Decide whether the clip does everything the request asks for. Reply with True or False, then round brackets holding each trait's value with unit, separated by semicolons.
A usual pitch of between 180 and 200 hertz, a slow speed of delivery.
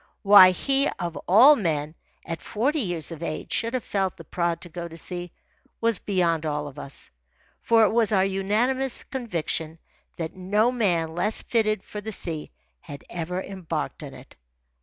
False (185 Hz; 175 wpm)